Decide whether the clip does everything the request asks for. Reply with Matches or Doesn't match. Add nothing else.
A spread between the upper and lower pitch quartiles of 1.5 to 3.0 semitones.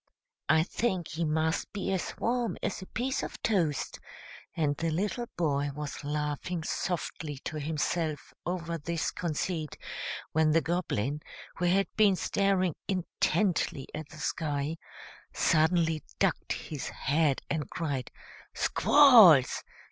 Doesn't match